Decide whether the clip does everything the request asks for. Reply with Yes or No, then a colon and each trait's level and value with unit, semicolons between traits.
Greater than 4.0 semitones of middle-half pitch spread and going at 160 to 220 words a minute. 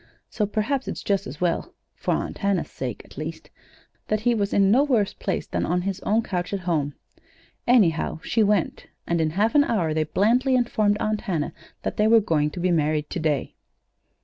Yes: average, 5.1 semitones; average, 200 wpm